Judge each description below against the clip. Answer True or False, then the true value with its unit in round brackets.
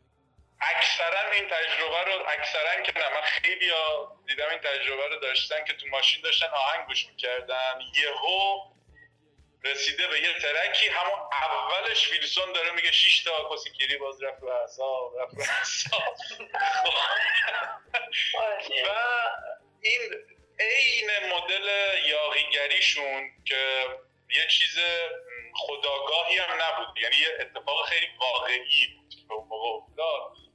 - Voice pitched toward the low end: False (160 Hz)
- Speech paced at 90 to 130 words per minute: True (110 wpm)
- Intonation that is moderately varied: False (7.7 semitones)